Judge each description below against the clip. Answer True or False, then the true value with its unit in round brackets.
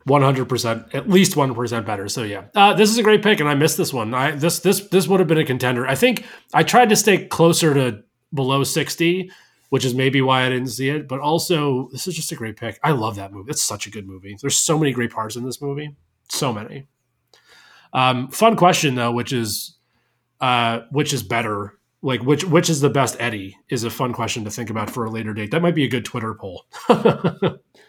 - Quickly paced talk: True (235 wpm)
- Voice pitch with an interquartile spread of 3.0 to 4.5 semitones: False (5.3 semitones)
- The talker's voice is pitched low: True (130 Hz)